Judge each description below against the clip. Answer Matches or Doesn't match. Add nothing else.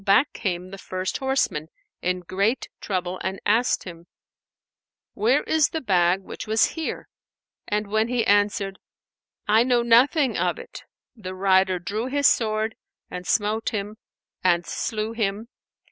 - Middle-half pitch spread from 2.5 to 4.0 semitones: Matches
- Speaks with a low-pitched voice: Doesn't match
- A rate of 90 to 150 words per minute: Matches